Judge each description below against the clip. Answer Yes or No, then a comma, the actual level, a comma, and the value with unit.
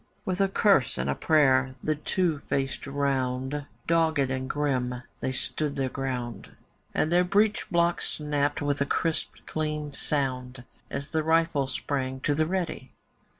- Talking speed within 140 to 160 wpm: Yes, average, 150 wpm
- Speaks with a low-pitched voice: No, medium, 145 Hz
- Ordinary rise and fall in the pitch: Yes, average, 3.3 semitones